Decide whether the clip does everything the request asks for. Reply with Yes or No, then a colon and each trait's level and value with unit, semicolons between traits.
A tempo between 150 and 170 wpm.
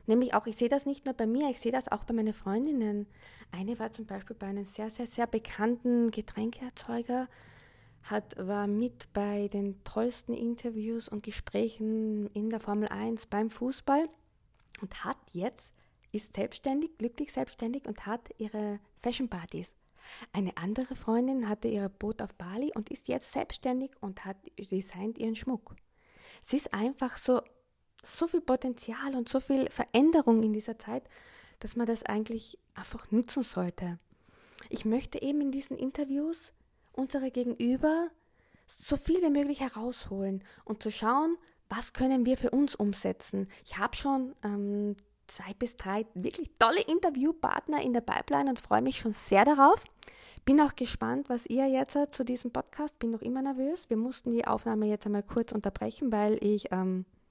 Yes: average, 165 wpm